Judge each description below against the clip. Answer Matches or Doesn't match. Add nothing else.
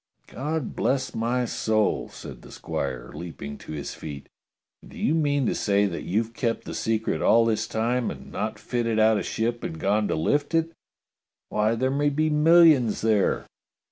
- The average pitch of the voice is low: Matches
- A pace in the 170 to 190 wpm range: Matches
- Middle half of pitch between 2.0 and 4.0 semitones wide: Doesn't match